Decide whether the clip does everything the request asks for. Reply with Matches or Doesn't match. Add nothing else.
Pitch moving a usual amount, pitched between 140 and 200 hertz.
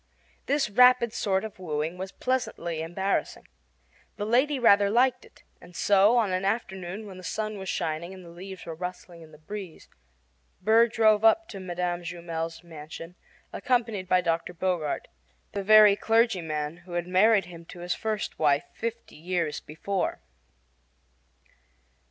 Matches